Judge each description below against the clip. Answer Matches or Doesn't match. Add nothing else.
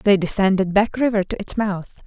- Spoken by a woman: Matches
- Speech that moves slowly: Doesn't match